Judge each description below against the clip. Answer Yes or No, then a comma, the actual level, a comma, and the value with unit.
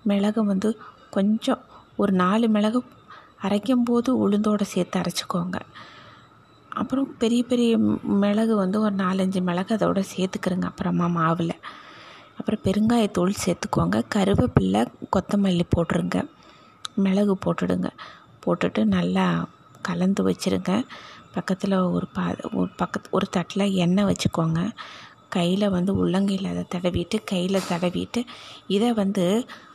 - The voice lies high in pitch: Yes, high, 195 Hz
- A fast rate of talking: No, average, 105 wpm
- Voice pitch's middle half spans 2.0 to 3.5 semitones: Yes, average, 3.0 semitones